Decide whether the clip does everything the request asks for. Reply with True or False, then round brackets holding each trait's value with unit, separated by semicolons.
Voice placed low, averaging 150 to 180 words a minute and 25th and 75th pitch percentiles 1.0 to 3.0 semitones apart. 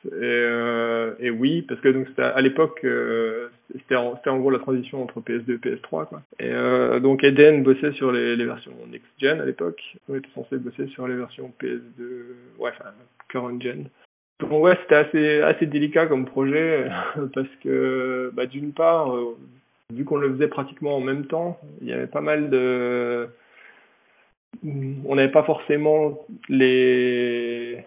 False (130 Hz; 170 wpm; 3.4 semitones)